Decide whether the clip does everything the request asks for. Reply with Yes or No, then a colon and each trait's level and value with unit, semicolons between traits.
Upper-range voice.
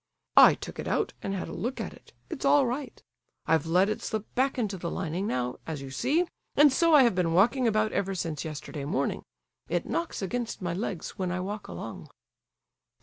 Yes: high, 200 Hz